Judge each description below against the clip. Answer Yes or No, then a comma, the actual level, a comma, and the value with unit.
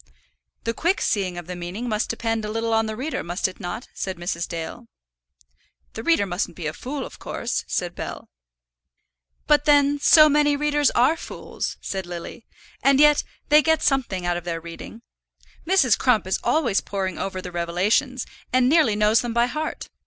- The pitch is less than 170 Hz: No, high, 225 Hz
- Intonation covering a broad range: Yes, wide, 7.5 semitones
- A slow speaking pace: No, average, 180 wpm